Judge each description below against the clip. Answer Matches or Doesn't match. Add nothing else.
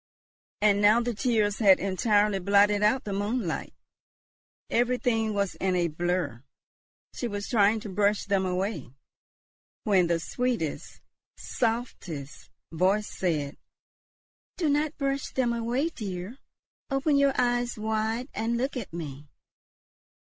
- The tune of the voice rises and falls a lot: Doesn't match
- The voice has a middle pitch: Doesn't match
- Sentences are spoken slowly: Matches